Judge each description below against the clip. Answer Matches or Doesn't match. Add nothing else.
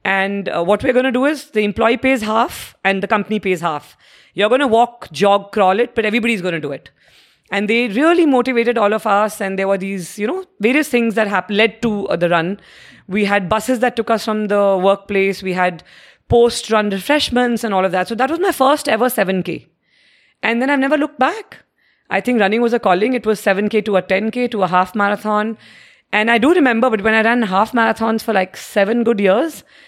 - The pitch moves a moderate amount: Matches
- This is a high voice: Matches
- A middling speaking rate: Doesn't match